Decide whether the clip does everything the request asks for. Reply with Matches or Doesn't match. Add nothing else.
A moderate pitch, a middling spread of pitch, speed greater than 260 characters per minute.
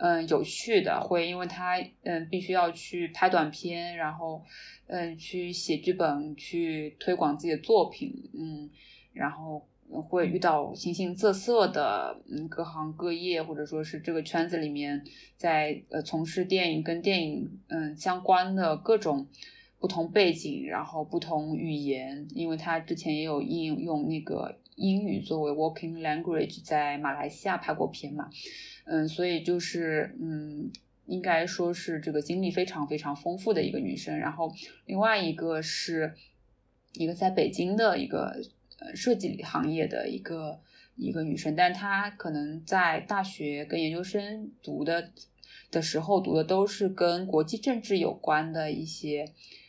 Doesn't match